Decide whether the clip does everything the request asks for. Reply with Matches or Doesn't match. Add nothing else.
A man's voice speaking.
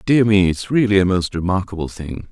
Matches